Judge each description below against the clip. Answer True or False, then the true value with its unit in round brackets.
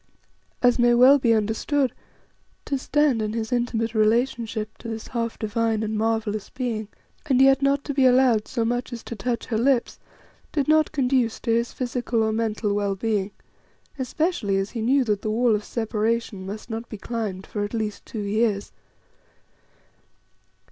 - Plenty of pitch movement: False (2.6 semitones)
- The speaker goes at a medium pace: True (170 wpm)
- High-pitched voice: True (230 Hz)